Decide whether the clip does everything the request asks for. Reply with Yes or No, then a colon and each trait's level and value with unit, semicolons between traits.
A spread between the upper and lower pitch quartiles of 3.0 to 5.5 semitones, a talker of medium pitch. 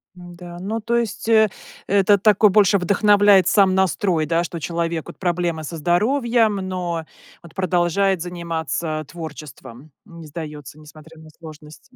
Yes: average, 3.7 semitones; medium, 175 Hz